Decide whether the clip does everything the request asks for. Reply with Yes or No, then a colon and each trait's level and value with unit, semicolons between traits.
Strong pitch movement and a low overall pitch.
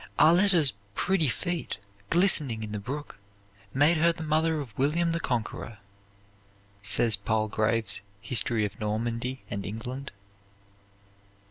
Yes: wide, 6.6 semitones; low, 125 Hz